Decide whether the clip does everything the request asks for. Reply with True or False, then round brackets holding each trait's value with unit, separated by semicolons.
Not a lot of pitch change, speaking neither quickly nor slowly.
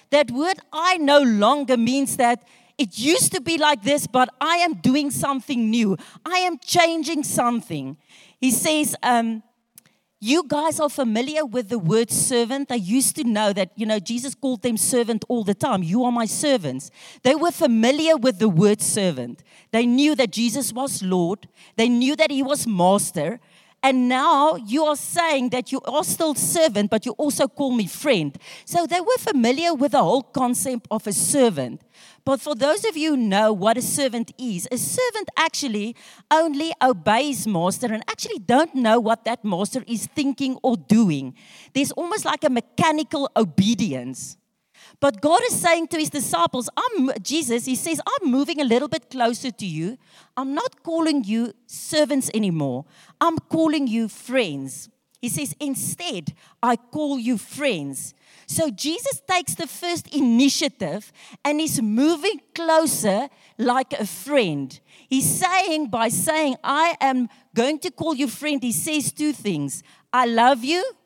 False (5.3 semitones; 170 wpm)